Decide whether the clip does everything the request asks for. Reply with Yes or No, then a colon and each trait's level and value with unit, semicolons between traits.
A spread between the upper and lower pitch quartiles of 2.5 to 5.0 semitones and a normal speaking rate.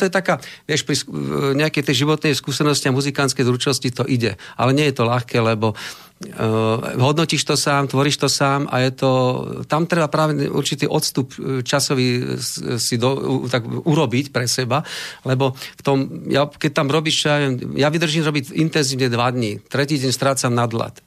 No: average, 2.8 semitones; fast, 170 wpm